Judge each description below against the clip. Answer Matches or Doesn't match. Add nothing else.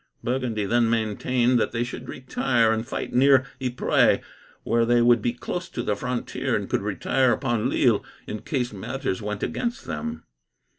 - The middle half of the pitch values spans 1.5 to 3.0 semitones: Matches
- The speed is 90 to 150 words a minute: Doesn't match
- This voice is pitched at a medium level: Doesn't match